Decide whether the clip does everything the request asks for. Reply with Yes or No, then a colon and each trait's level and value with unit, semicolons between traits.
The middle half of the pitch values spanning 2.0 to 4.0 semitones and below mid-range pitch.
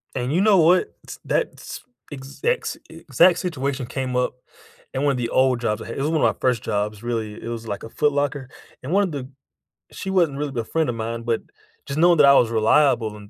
No: average, 4.5 semitones; low, 130 Hz